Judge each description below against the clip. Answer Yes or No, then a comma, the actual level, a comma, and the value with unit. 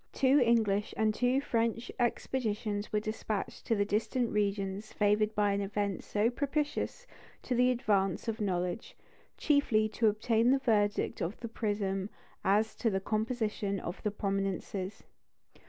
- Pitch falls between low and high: No, high, 215 Hz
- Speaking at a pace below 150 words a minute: Yes, average, 140 wpm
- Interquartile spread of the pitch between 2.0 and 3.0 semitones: Yes, narrow, 2.5 semitones